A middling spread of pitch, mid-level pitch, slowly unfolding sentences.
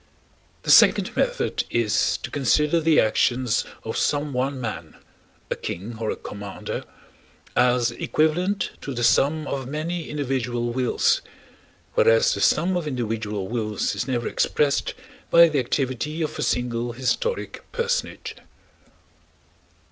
No: average, 5.0 semitones; low, 130 Hz; slow, 125 wpm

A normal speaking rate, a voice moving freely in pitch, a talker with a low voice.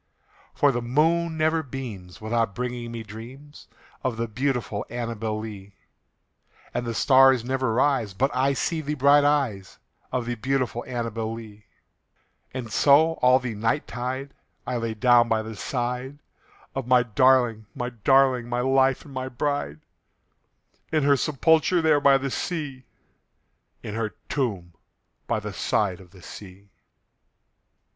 No: average, 145 wpm; average, 3.5 semitones; low, 125 Hz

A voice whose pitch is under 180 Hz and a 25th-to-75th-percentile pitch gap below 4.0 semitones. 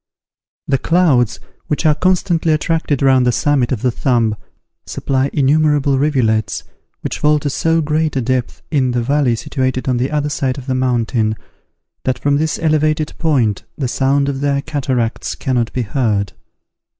Yes: low, 135 Hz; average, 3.3 semitones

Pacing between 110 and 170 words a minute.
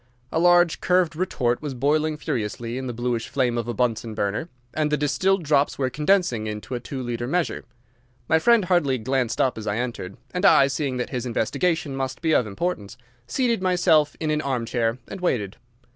No: average, 190 wpm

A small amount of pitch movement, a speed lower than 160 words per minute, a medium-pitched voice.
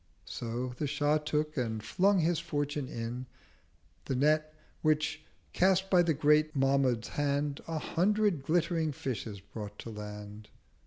No: average, 4.2 semitones; average, 140 wpm; medium, 145 Hz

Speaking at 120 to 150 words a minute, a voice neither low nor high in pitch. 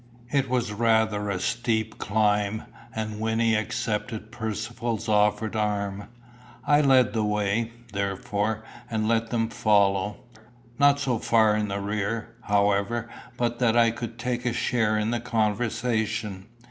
No: average, 140 wpm; low, 110 Hz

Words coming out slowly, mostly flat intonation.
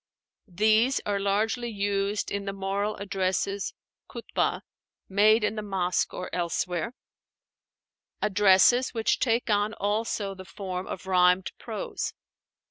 Yes: slow, 120 wpm; narrow, 2.1 semitones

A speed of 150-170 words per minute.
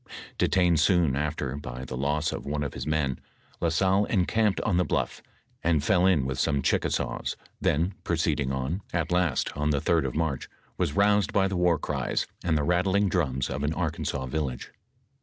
No: average, 185 wpm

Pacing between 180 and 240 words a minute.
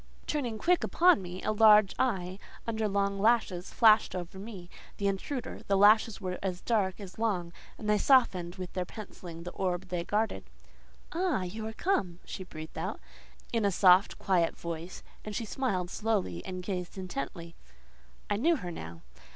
No: average, 170 wpm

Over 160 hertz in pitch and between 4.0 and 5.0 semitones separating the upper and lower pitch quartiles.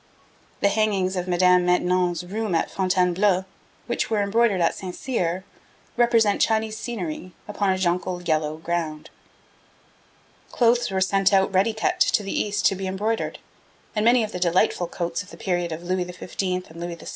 No: medium, 185 Hz; average, 2.9 semitones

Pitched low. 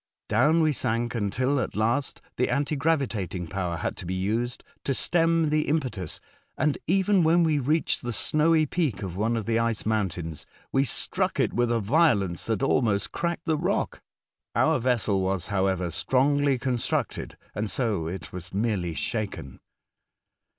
Yes: low, 120 Hz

